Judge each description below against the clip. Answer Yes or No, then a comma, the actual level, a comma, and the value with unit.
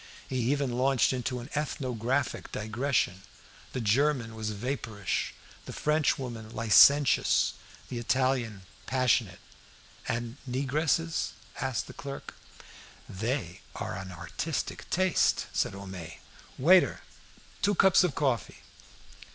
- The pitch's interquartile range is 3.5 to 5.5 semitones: Yes, average, 4.1 semitones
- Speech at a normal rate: No, slow, 110 wpm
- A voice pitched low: Yes, low, 125 Hz